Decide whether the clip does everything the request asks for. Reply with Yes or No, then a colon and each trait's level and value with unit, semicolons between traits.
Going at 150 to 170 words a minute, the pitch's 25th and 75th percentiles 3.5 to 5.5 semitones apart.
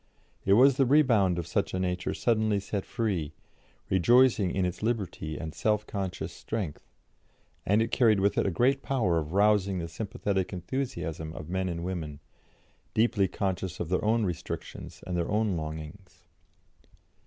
Yes: average, 160 wpm; average, 3.9 semitones